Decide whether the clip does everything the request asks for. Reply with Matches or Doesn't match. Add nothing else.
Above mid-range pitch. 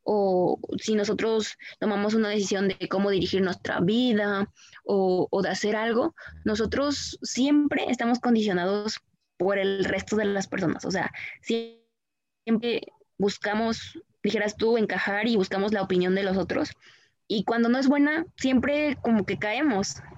Matches